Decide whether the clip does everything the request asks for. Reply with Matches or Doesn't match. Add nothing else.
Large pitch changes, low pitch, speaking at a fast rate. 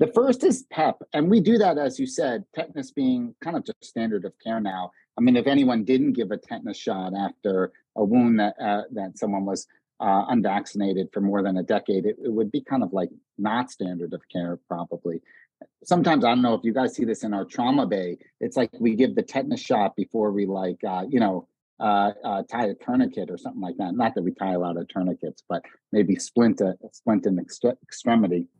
Matches